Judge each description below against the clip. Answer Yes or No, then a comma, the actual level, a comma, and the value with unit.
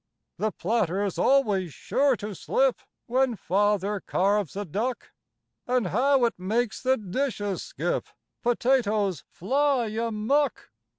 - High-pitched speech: Yes, high, 220 Hz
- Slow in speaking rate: Yes, slow, 115 wpm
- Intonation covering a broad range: No, average, 4.4 semitones